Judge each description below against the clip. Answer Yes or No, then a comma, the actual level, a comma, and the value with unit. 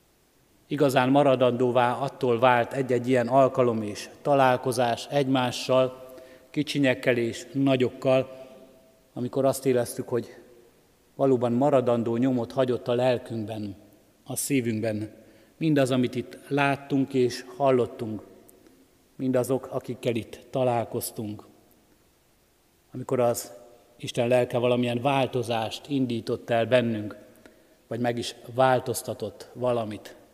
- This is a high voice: No, low, 125 Hz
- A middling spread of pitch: No, narrow, 1.8 semitones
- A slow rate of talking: Yes, slow, 95 wpm